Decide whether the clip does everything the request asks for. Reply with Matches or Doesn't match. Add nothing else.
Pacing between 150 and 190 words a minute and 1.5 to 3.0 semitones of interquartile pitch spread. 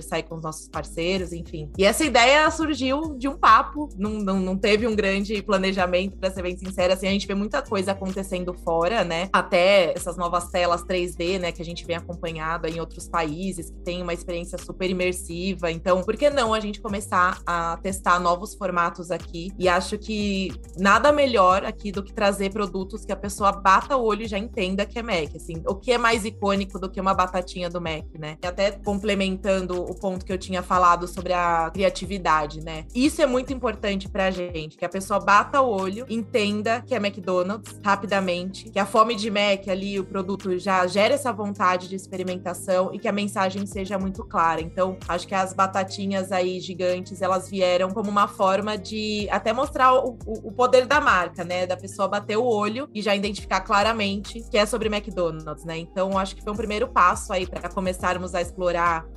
Doesn't match